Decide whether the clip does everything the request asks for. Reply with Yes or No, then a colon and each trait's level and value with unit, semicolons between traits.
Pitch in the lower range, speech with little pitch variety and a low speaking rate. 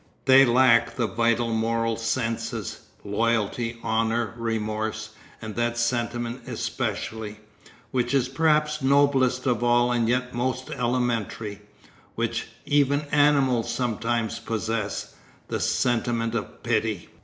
Yes: low, 115 Hz; narrow, 2.0 semitones; slow, 110 wpm